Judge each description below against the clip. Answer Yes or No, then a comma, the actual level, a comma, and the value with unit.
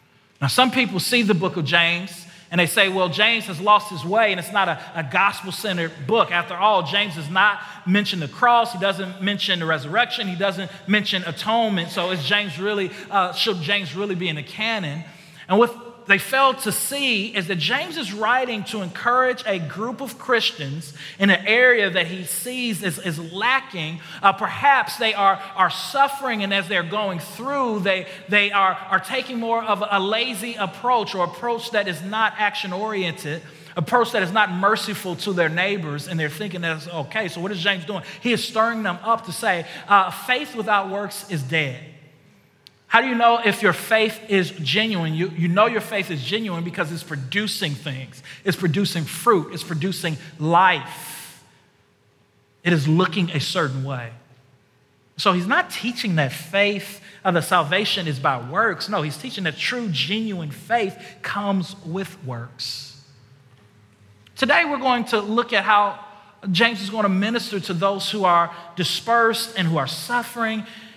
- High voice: Yes, high, 195 Hz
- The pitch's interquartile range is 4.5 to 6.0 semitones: No, average, 4.1 semitones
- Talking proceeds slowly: No, average, 180 wpm